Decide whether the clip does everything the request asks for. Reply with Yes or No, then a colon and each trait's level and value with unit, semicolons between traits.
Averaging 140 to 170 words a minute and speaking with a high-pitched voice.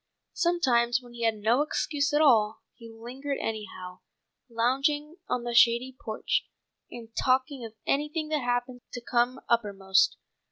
Yes: average, 145 wpm; high, 245 Hz